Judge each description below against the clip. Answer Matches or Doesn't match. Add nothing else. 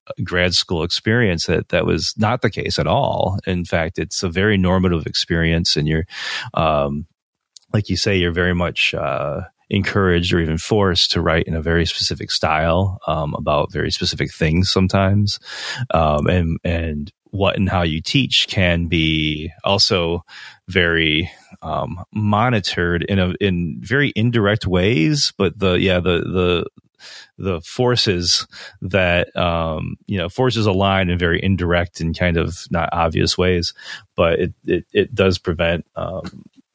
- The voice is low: Matches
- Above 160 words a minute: Doesn't match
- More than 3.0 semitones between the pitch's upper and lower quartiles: Doesn't match